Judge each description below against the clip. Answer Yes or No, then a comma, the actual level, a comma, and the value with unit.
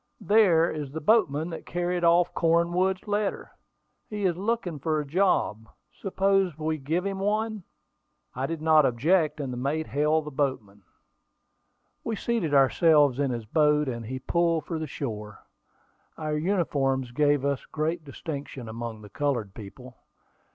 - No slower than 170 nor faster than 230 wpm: No, average, 150 wpm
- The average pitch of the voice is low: No, medium, 155 Hz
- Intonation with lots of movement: No, average, 4.5 semitones